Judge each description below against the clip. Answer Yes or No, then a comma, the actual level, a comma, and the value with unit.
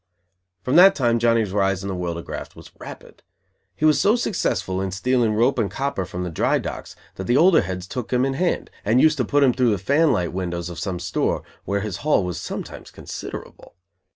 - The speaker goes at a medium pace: No, fast, 220 wpm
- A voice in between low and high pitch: No, low, 110 Hz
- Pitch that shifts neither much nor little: No, wide, 6.4 semitones